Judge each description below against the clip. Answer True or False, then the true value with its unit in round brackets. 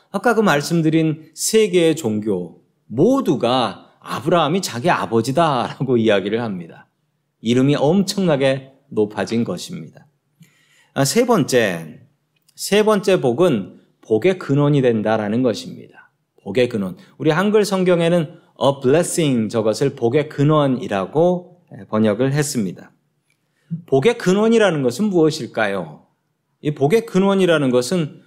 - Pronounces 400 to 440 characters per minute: False (280 characters per minute)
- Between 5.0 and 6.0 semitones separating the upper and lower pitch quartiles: True (5.6 semitones)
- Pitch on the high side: False (155 Hz)